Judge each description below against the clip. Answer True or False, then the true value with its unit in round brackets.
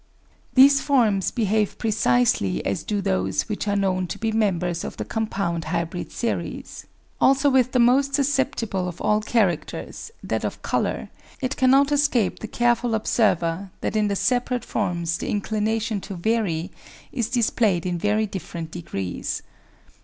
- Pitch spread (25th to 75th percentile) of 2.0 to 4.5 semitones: False (5.2 semitones)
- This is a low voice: False (210 Hz)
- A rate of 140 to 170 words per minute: True (155 wpm)